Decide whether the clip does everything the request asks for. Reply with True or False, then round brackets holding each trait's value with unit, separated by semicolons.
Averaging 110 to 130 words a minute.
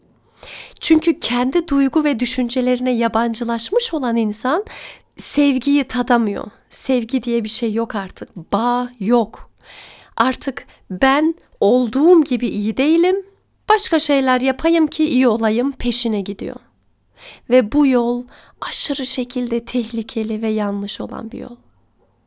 True (115 wpm)